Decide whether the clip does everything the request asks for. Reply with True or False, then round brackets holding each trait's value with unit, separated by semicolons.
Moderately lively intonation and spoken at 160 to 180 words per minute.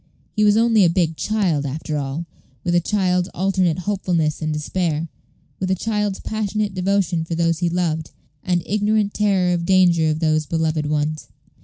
True (3.7 semitones; 170 wpm)